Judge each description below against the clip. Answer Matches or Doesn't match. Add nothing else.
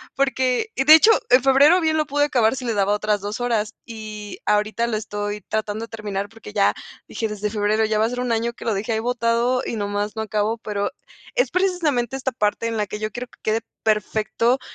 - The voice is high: Matches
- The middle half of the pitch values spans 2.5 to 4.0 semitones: Matches